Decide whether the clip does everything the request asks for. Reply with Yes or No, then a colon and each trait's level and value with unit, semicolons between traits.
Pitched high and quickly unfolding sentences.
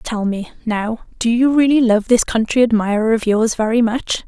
No: high, 230 Hz; average, 195 wpm